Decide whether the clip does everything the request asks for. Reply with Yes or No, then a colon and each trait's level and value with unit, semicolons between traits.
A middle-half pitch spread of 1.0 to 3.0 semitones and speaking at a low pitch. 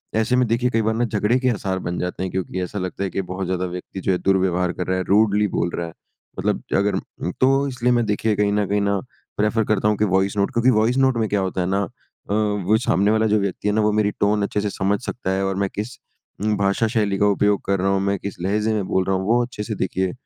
Yes: narrow, 2.4 semitones; low, 100 Hz